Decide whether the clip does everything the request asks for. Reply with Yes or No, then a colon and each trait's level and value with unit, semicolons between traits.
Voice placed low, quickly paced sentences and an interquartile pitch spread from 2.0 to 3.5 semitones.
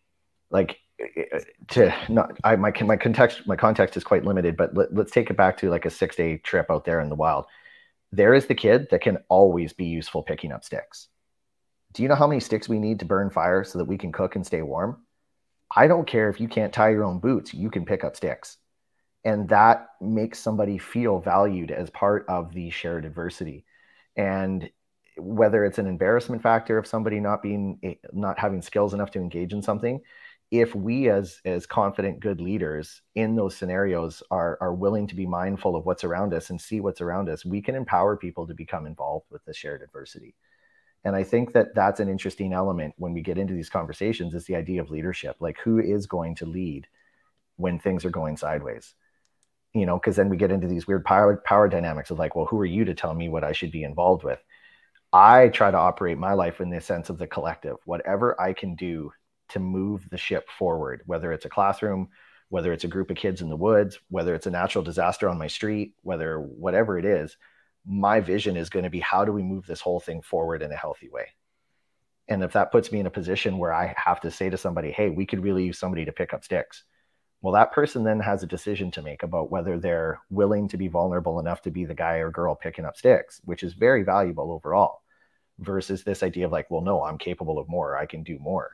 Yes: very low, 95 Hz; fast, 225 wpm; average, 3.1 semitones